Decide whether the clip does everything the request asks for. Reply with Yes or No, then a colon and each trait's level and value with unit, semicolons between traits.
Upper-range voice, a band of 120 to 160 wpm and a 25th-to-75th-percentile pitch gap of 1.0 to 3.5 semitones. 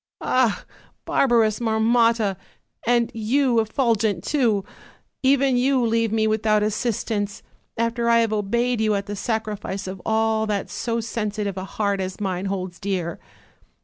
Yes: high, 220 Hz; average, 145 wpm; narrow, 2.6 semitones